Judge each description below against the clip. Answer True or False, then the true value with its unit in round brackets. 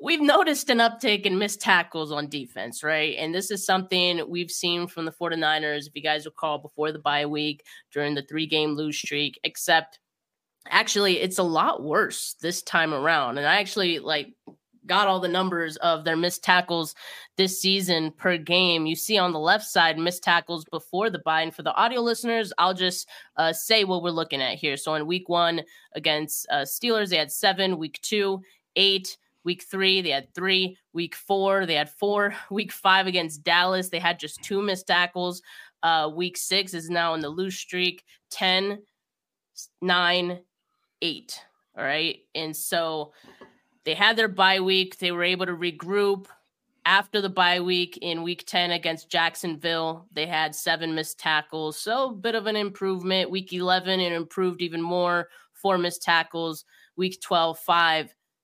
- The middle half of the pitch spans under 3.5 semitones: True (3.0 semitones)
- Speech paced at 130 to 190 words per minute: True (180 wpm)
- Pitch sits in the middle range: True (175 Hz)